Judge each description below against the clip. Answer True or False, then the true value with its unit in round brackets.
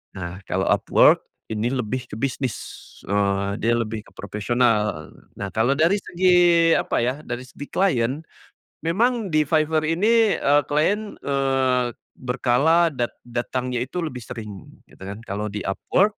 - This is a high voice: False (125 Hz)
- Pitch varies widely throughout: True (6.6 semitones)